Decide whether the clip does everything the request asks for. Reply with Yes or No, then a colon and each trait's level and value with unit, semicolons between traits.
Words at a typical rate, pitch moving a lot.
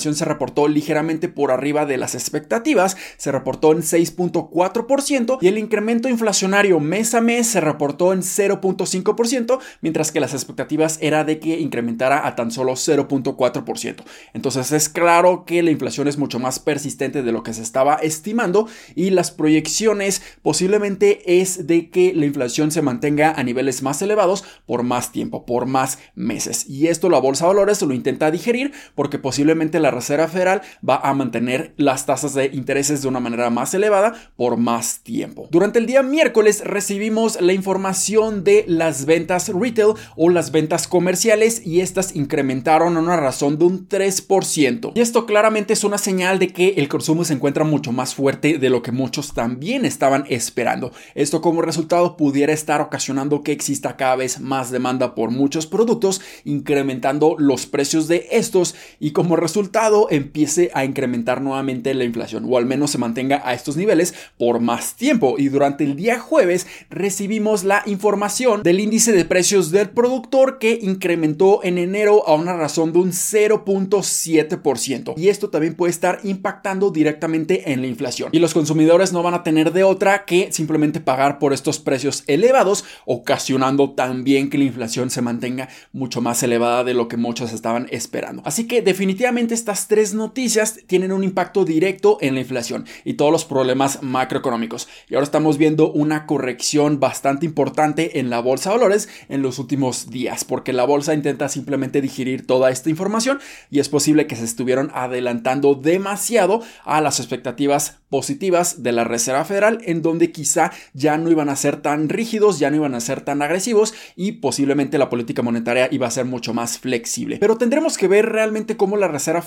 Yes: average, 175 wpm; wide, 5.9 semitones